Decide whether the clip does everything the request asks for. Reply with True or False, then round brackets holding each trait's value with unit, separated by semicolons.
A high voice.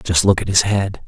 False (95 Hz)